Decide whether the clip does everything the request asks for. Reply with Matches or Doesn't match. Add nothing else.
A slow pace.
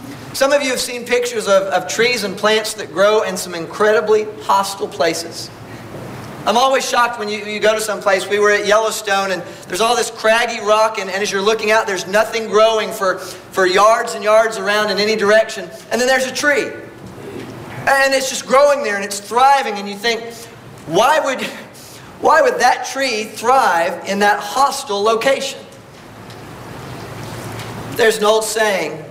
Doesn't match